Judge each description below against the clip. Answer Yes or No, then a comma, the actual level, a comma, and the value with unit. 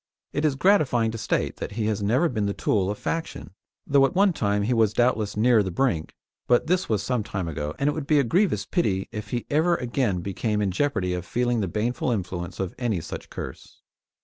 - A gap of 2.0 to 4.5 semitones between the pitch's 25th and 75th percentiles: No, average, 5.3 semitones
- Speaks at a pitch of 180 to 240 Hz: No, low, 115 Hz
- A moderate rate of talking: No, fast, 225 wpm